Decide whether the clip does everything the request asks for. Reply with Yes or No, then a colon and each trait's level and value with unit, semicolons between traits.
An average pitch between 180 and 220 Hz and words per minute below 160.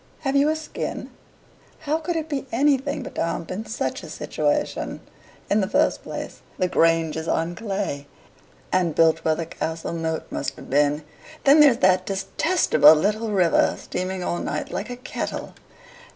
No: high, 190 Hz; average, 165 wpm